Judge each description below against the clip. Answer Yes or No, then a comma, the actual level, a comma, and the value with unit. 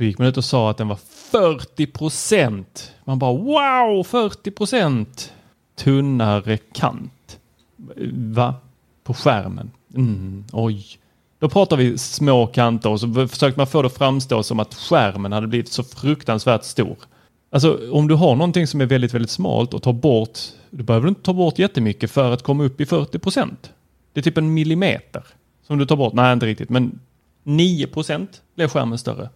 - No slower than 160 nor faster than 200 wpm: Yes, average, 175 wpm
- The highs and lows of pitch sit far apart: No, average, 4.8 semitones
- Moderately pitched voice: No, low, 130 Hz